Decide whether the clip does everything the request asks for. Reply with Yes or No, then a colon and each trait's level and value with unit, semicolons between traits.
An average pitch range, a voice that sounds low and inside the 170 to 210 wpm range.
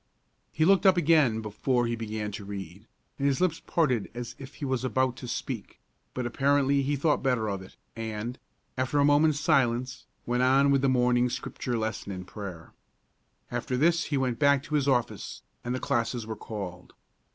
Yes: average, 4.0 semitones; low, 125 Hz; average, 185 wpm